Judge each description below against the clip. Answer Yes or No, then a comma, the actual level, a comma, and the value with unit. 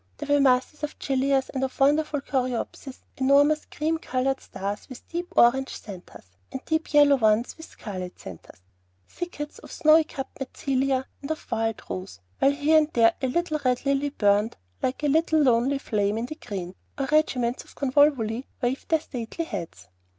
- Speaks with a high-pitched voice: Yes, very high, 270 Hz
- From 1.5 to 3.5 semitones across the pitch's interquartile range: No, average, 4.3 semitones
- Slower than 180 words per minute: Yes, average, 170 wpm